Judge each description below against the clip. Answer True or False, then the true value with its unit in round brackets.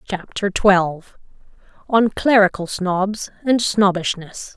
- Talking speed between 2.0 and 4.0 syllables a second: True (3.7 syllables/s)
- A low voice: False (195 Hz)